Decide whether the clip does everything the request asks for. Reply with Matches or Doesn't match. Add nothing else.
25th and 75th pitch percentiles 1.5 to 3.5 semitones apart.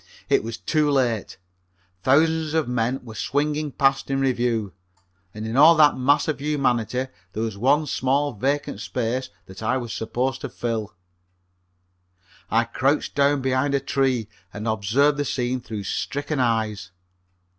Doesn't match